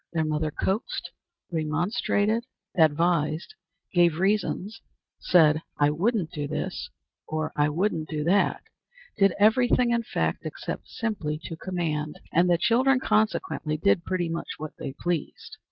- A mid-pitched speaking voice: Yes, medium, 170 Hz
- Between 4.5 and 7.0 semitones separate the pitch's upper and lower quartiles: Yes, average, 5.2 semitones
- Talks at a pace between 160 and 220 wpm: No, slow, 135 wpm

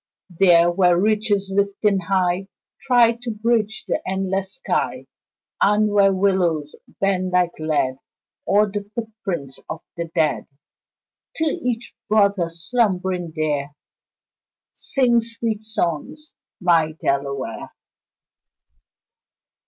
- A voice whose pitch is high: Yes, high, 195 Hz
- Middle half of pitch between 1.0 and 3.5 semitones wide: No, average, 4.1 semitones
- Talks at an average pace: No, slow, 100 wpm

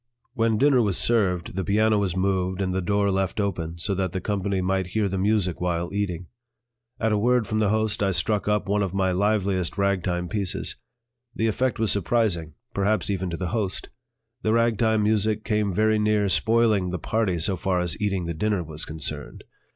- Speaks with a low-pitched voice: Yes, low, 100 Hz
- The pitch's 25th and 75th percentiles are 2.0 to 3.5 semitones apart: Yes, average, 2.9 semitones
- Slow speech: No, average, 195 wpm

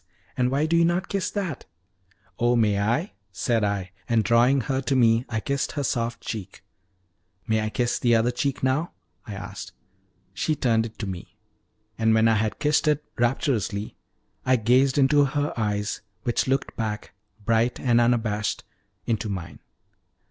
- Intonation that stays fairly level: No, average, 3.9 semitones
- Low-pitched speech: Yes, low, 120 Hz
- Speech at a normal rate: Yes, average, 165 wpm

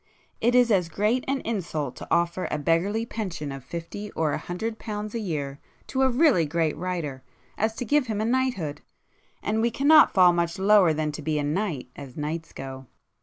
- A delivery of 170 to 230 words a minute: Yes, average, 195 wpm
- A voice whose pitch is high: No, medium, 180 Hz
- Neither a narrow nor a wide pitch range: No, wide, 6.4 semitones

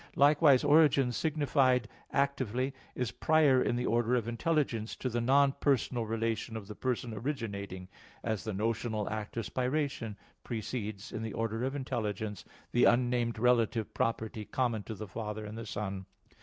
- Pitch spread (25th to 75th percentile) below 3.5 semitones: Yes, average, 3.1 semitones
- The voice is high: No, low, 115 Hz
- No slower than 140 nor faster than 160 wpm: Yes, average, 155 wpm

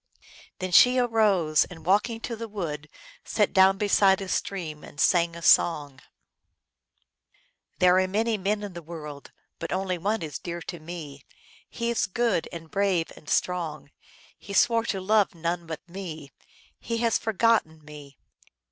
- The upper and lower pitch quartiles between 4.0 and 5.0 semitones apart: Yes, average, 4.5 semitones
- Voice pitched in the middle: Yes, medium, 180 Hz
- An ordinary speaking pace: Yes, average, 160 wpm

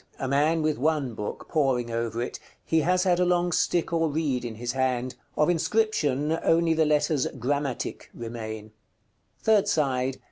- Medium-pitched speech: Yes, medium, 145 Hz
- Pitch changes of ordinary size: Yes, average, 4.7 semitones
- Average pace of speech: Yes, average, 170 wpm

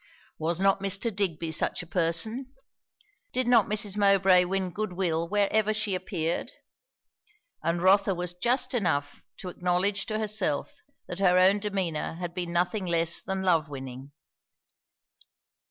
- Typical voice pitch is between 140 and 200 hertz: Yes, medium, 185 Hz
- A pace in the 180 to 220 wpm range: No, average, 140 wpm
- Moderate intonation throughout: Yes, average, 3.1 semitones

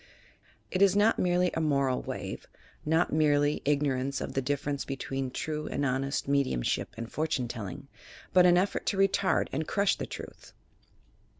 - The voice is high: No, medium, 145 Hz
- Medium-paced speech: Yes, average, 165 wpm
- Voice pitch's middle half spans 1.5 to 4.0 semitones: No, average, 4.7 semitones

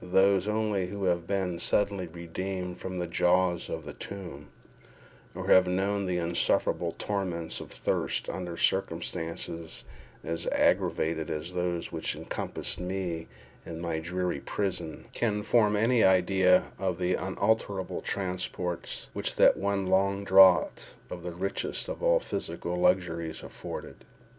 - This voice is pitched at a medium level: No, very low, 90 Hz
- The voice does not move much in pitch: Yes, narrow, 2.3 semitones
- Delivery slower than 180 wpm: Yes, average, 140 wpm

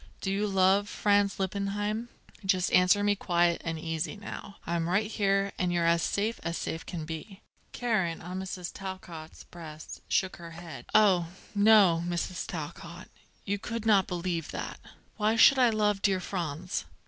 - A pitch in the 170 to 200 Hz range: Yes, high, 190 Hz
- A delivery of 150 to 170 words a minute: Yes, average, 160 wpm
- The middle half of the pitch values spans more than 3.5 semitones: No, average, 3.1 semitones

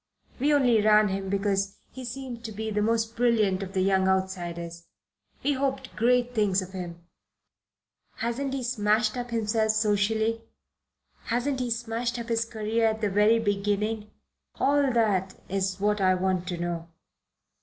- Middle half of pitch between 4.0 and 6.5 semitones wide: No, average, 3.4 semitones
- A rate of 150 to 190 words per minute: Yes, average, 155 wpm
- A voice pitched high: Yes, high, 215 Hz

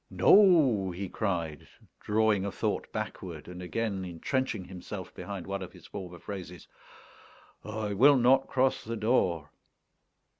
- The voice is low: Yes, low, 100 Hz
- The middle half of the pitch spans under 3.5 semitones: No, average, 4.2 semitones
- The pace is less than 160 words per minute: Yes, slow, 135 wpm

